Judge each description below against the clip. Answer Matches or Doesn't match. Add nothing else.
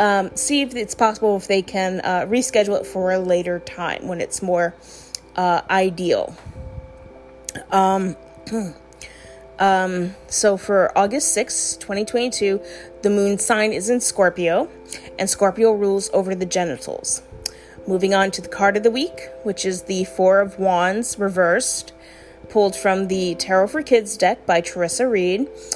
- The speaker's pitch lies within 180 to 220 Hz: Matches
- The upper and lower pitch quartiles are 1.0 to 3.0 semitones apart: Matches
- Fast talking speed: Doesn't match